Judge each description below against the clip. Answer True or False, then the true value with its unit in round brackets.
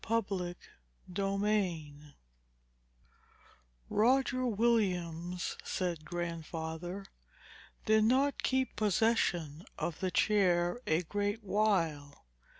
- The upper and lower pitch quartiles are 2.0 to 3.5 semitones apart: False (4.2 semitones)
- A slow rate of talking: True (75 wpm)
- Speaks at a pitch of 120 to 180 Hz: False (190 Hz)